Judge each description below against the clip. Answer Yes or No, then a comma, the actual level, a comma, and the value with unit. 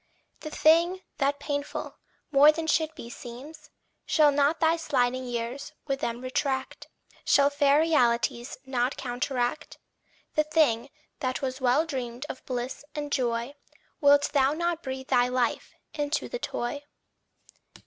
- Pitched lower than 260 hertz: No, very high, 275 Hz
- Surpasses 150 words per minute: No, average, 140 wpm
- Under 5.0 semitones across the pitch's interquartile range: Yes, average, 3.4 semitones